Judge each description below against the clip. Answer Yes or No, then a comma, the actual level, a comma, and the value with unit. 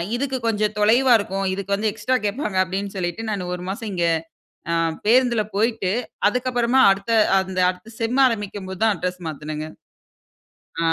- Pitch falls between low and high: No, high, 210 Hz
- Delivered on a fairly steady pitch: No, average, 3.7 semitones